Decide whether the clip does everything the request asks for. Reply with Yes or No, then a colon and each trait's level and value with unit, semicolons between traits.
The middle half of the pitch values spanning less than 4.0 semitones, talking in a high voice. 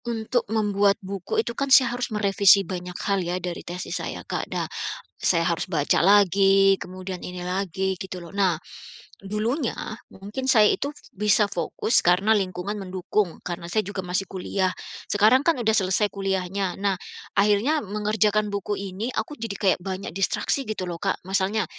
Yes: narrow, 2.4 semitones; high, 200 Hz